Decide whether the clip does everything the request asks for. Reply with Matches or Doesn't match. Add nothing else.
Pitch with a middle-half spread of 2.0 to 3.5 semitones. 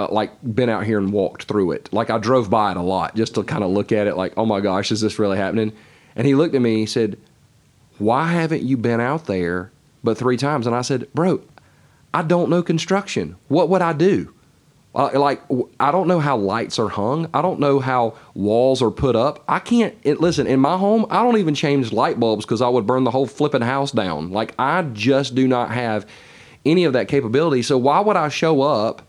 Doesn't match